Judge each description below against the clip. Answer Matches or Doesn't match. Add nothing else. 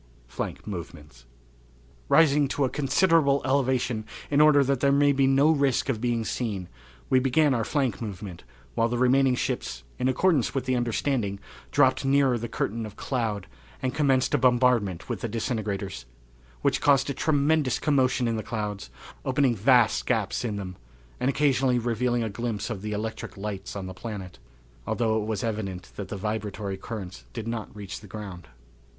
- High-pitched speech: Doesn't match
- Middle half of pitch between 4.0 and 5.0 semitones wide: Matches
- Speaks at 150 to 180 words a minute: Matches